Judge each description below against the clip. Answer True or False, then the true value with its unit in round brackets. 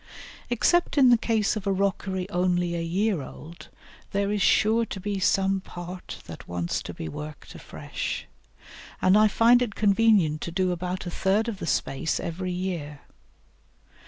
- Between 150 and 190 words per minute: True (165 wpm)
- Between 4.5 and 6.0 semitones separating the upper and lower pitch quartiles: False (3.4 semitones)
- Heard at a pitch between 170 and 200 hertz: True (190 Hz)